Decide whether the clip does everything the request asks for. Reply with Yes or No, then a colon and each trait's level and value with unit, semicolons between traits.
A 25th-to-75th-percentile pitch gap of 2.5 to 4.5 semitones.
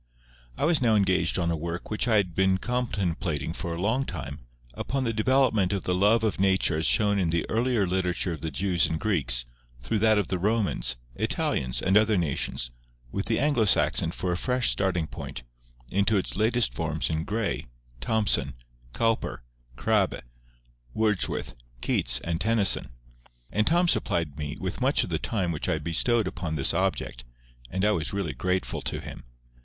No: average, 5.0 semitones